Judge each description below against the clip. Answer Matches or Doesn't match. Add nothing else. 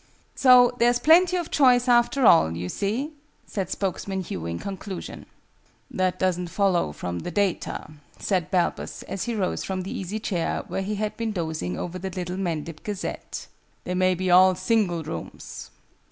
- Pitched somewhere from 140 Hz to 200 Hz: Matches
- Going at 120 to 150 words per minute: Doesn't match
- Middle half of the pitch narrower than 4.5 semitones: Matches